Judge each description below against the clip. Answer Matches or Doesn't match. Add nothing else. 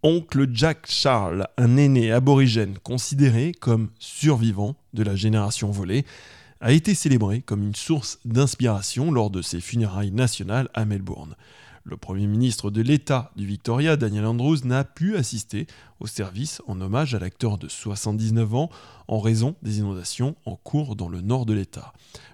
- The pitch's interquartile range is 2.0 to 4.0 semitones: Doesn't match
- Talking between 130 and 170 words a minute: Matches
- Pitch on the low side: Matches